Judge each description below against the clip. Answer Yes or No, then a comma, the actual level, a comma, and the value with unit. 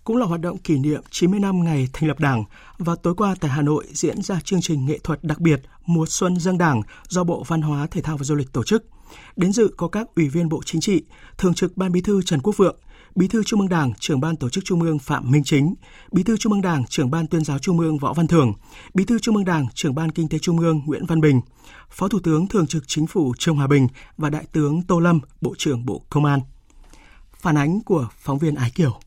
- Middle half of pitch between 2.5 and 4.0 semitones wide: Yes, average, 3.5 semitones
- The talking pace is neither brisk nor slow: No, fast, 260 wpm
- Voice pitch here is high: No, medium, 160 Hz